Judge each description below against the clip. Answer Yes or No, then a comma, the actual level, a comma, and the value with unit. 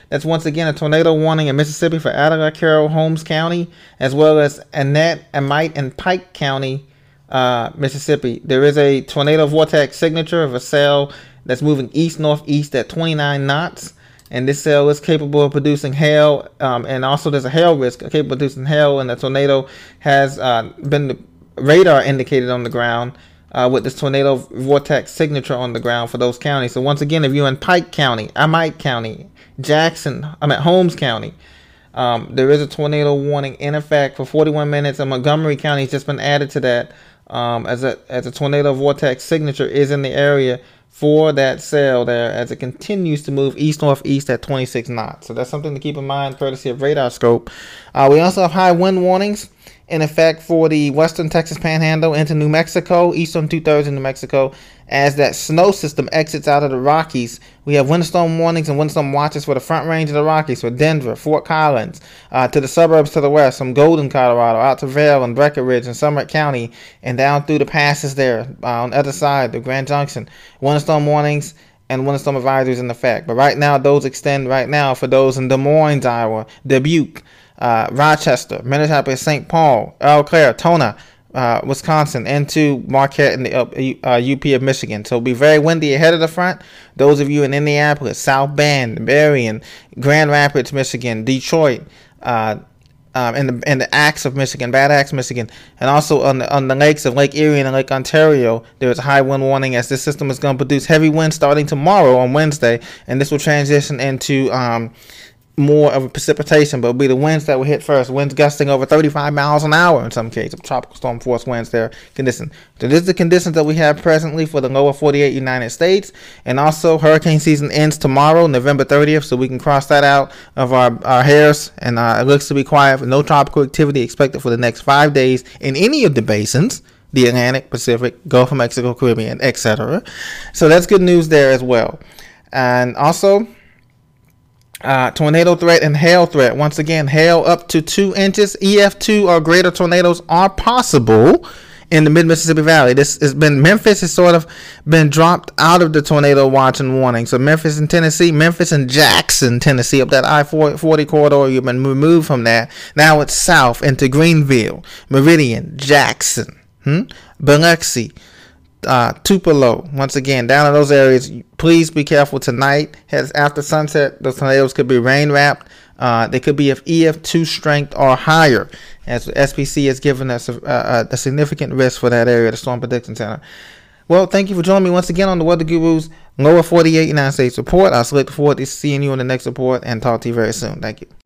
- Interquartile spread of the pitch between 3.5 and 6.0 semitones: No, average, 3.0 semitones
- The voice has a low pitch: No, medium, 145 Hz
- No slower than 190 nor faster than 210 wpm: Yes, average, 200 wpm